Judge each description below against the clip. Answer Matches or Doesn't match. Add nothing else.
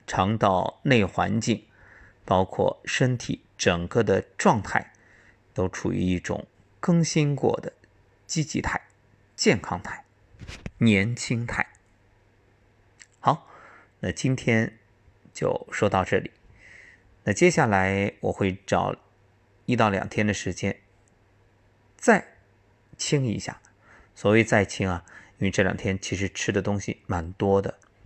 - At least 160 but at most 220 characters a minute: Matches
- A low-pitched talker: Matches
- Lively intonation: Doesn't match